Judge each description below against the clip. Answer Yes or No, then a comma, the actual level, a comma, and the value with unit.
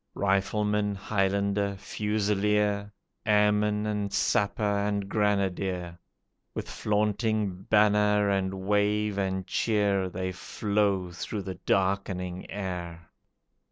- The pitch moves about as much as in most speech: No, narrow, 1.5 semitones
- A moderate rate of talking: No, slow, 90 wpm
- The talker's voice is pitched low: Yes, low, 100 Hz